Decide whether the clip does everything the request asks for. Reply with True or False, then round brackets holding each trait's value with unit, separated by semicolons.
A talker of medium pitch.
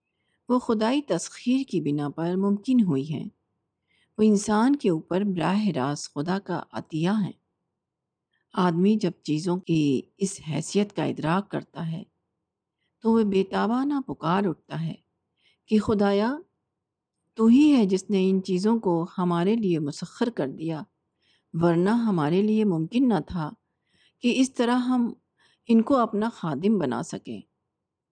False (195 Hz)